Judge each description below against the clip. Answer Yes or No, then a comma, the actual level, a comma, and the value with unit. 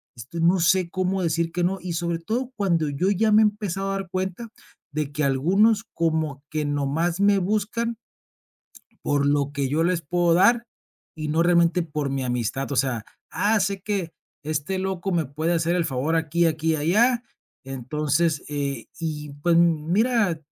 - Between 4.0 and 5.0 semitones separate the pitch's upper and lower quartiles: Yes, average, 4.3 semitones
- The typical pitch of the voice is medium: Yes, medium, 170 Hz